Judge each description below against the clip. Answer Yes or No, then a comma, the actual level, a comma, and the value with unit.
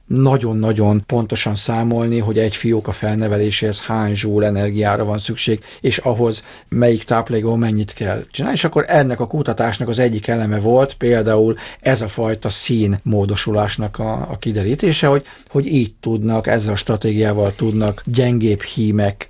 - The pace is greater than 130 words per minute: Yes, average, 150 wpm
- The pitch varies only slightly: Yes, narrow, 2.0 semitones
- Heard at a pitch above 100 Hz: Yes, low, 110 Hz